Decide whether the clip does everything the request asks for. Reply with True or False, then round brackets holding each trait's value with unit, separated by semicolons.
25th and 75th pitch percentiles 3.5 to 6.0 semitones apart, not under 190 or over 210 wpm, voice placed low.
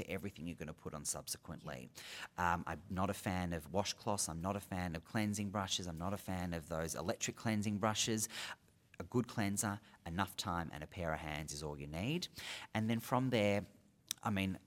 True (3.8 semitones; 205 wpm; 95 Hz)